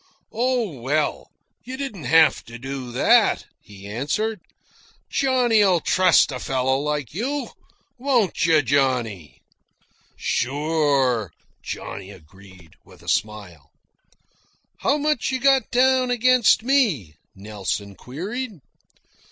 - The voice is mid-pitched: Yes, medium, 150 Hz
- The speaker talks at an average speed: No, slow, 105 wpm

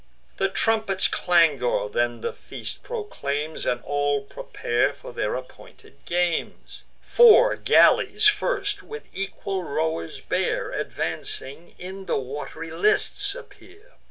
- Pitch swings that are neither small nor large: No, wide, 8.1 semitones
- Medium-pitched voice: Yes, medium, 170 Hz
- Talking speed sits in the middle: No, slow, 115 wpm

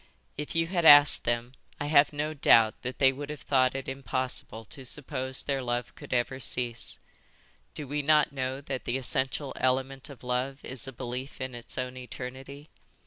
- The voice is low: Yes, low, 130 Hz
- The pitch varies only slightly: Yes, narrow, 2.1 semitones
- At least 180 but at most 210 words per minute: Yes, average, 185 wpm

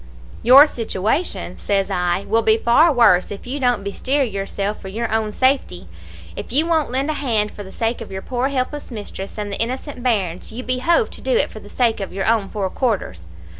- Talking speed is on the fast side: Yes, fast, 210 wpm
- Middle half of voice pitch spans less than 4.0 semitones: No, average, 4.6 semitones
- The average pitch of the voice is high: Yes, high, 225 Hz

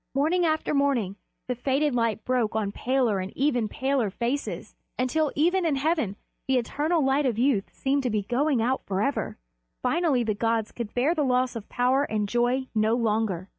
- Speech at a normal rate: Yes, average, 180 wpm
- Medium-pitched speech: No, very high, 250 Hz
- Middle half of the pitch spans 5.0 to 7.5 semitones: No, average, 4.1 semitones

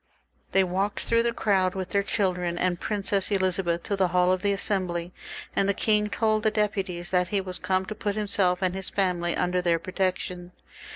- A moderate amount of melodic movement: No, narrow, 2.0 semitones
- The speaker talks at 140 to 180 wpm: No, average, 195 wpm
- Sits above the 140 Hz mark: Yes, high, 190 Hz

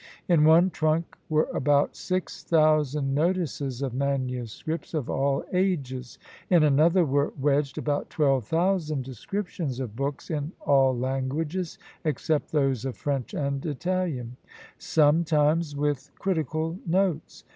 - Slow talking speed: Yes, slow, 125 wpm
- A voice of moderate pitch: Yes, medium, 150 Hz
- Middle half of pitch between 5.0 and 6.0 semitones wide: No, average, 3.3 semitones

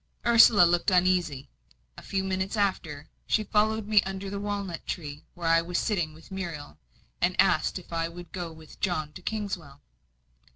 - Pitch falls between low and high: Yes, medium, 180 Hz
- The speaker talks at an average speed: Yes, average, 175 wpm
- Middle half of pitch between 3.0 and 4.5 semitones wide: Yes, average, 3.4 semitones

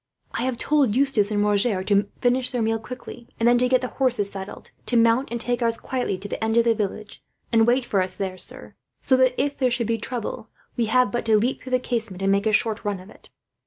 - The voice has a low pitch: No, high, 230 Hz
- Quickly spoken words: Yes, fast, 255 wpm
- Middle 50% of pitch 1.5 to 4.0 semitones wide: Yes, average, 3.3 semitones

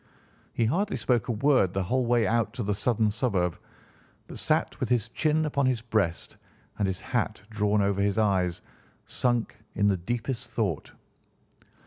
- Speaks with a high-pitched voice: No, low, 110 Hz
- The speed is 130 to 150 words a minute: No, average, 165 wpm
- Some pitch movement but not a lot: Yes, average, 3.4 semitones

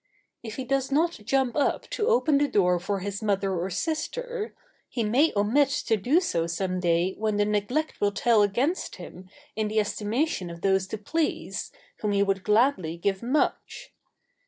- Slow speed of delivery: No, average, 180 wpm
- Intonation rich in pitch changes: Yes, wide, 6.3 semitones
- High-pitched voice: Yes, high, 210 Hz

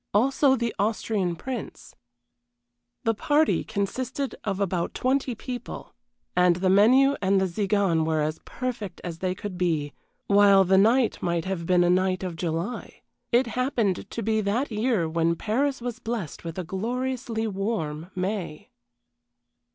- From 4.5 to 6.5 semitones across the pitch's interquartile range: Yes, average, 5.0 semitones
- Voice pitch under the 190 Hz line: No, high, 200 Hz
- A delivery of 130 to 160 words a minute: Yes, average, 150 wpm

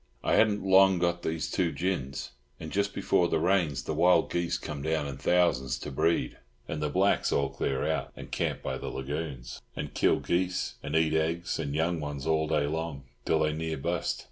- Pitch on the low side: Yes, very low, 80 Hz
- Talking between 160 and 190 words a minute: No, average, 200 wpm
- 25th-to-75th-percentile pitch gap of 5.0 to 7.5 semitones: No, average, 3.2 semitones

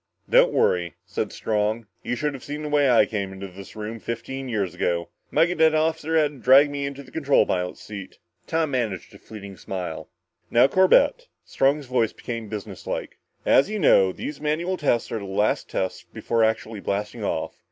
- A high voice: No, low, 120 Hz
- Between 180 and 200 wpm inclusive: Yes, average, 185 wpm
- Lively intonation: Yes, wide, 6.7 semitones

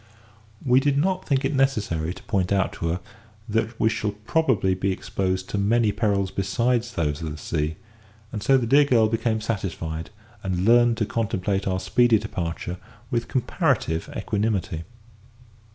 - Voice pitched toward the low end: Yes, low, 105 Hz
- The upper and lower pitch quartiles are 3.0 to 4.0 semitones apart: No, average, 4.4 semitones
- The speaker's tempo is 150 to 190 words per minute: Yes, average, 160 wpm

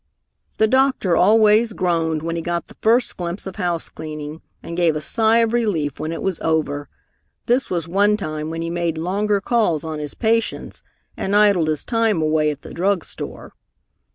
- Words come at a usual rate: Yes, average, 180 wpm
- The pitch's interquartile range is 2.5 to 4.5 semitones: No, average, 4.9 semitones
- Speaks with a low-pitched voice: No, medium, 175 Hz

